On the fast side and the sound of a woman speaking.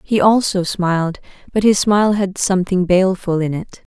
No: average, 165 wpm; female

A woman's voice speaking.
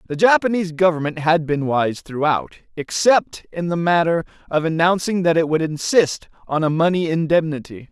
No: male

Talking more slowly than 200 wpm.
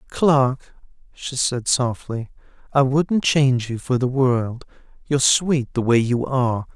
Yes: average, 150 wpm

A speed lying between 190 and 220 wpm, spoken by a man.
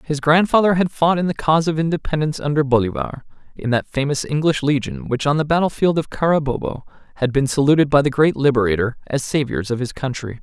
Yes: average, 195 wpm; male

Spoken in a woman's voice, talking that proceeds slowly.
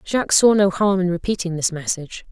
No: female; fast, 205 wpm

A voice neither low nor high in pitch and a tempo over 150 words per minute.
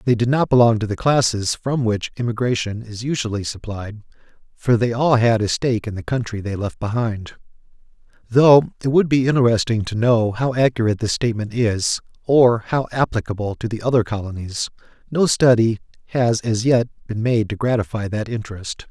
No: low, 115 Hz; average, 175 wpm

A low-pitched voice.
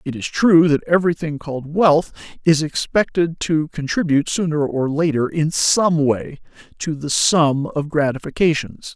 No: medium, 155 Hz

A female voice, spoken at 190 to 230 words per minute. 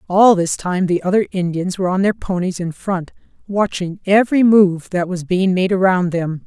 Yes: female; average, 195 wpm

